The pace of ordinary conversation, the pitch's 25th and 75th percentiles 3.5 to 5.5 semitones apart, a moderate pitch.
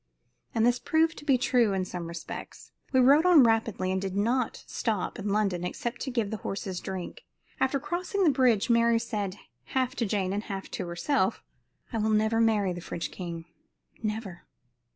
No: average, 185 wpm; average, 4.7 semitones; high, 220 Hz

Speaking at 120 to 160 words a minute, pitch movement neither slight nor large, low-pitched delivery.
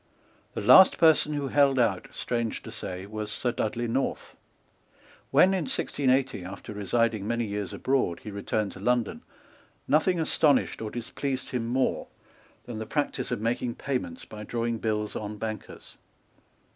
Yes: average, 150 wpm; average, 3.9 semitones; low, 115 Hz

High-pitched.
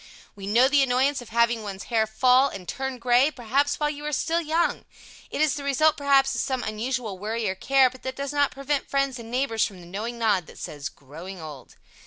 Yes: very high, 250 Hz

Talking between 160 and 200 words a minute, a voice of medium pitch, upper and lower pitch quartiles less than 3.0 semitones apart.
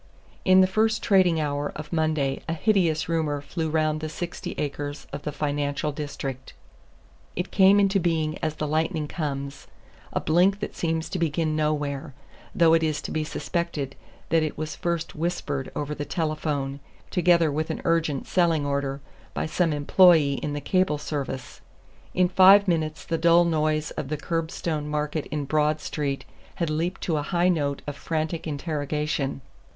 Yes: average, 165 wpm; medium, 155 Hz; narrow, 2.5 semitones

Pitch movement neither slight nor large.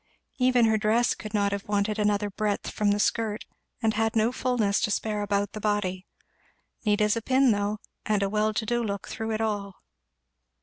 No: narrow, 1.5 semitones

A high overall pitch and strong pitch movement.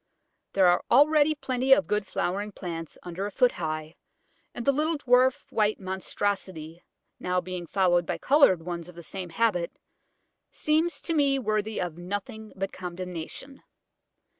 Yes: high, 195 Hz; wide, 6.5 semitones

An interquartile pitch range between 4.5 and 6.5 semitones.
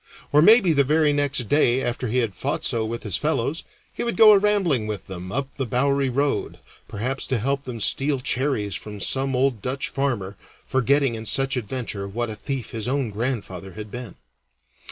No: average, 4.1 semitones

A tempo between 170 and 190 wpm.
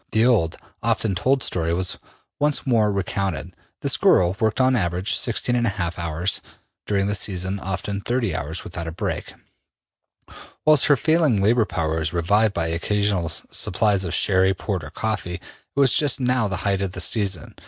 Yes: average, 175 wpm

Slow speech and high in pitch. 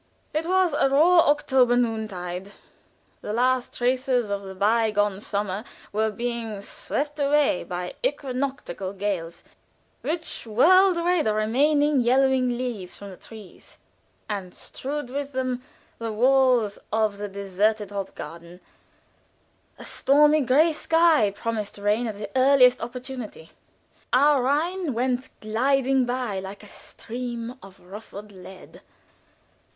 Yes: slow, 125 wpm; high, 240 Hz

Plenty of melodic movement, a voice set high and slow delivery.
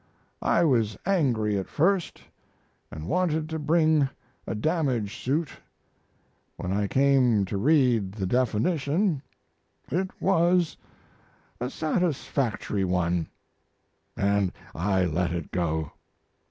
No: wide, 8.3 semitones; low, 125 Hz; slow, 105 wpm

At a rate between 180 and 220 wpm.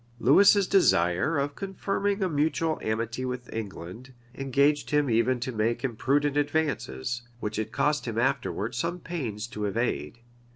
No: average, 150 wpm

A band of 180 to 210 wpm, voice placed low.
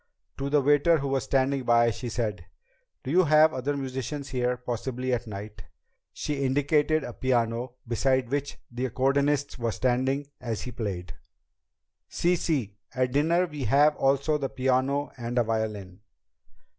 No: average, 155 wpm; low, 130 Hz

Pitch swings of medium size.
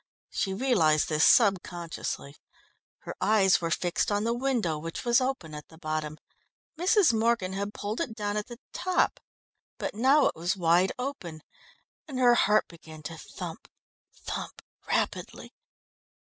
No: wide, 6.5 semitones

